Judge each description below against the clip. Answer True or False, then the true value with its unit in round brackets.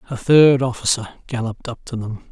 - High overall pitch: False (120 Hz)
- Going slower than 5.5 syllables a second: False (5.7 syllables/s)